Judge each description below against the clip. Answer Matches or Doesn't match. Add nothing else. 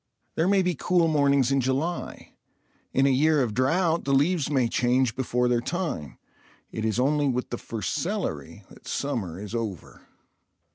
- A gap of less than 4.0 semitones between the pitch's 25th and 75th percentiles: Doesn't match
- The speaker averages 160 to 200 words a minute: Matches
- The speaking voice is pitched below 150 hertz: Matches